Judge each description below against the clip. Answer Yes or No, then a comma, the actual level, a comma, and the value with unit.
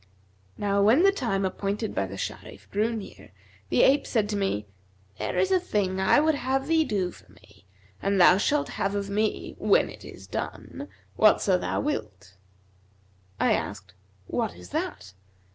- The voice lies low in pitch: No, high, 200 Hz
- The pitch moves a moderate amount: No, wide, 6.2 semitones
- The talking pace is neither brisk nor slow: Yes, average, 170 wpm